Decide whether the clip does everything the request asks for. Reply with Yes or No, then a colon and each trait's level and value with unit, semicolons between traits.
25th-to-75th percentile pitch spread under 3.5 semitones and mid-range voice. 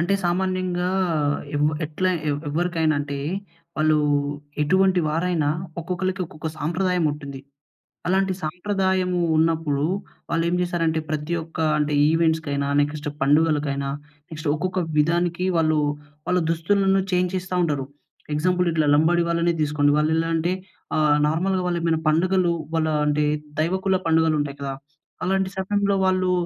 Yes: average, 3.0 semitones; medium, 165 Hz